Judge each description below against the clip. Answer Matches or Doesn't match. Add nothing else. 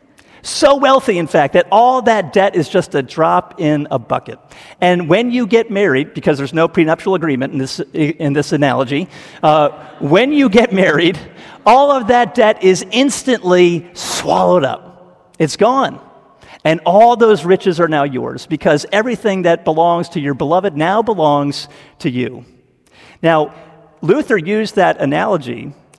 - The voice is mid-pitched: Matches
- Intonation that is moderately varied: Doesn't match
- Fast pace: Doesn't match